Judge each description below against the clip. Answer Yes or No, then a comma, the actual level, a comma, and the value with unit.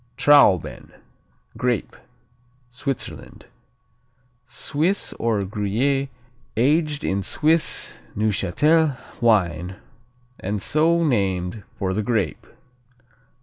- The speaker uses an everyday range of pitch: No, wide, 6.9 semitones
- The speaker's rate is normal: No, slow, 75 wpm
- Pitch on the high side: No, low, 115 Hz